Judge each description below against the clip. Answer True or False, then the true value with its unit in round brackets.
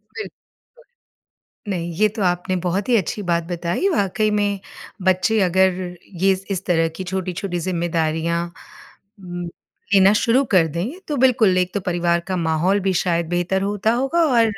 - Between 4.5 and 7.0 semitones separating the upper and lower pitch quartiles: False (3.0 semitones)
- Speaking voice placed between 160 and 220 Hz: True (185 Hz)